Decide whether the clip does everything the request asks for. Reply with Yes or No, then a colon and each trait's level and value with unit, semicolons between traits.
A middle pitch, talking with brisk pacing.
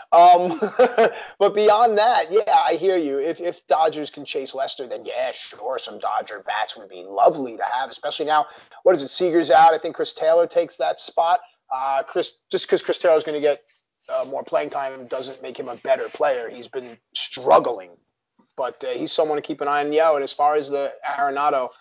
Yes: medium, 170 Hz; fast, 210 wpm